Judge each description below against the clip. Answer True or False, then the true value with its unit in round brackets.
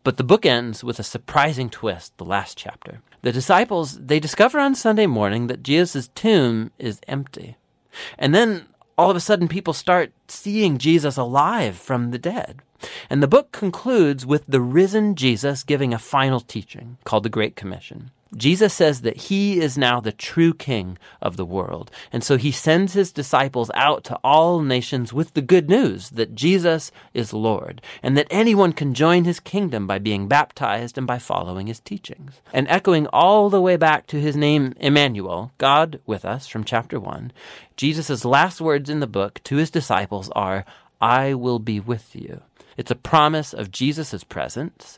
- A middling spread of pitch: False (5.8 semitones)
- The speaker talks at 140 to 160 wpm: False (180 wpm)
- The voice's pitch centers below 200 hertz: True (140 Hz)